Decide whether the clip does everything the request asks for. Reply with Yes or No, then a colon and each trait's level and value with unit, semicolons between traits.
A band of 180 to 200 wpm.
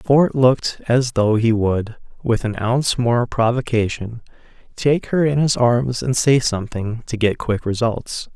No: average, 165 wpm